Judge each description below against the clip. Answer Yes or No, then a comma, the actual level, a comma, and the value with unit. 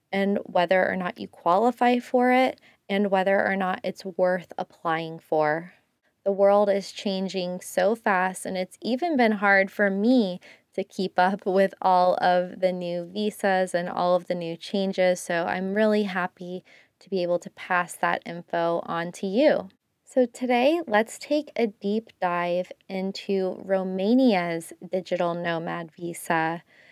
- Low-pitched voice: No, high, 190 Hz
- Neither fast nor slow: Yes, average, 155 wpm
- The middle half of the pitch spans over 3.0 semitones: No, narrow, 2.4 semitones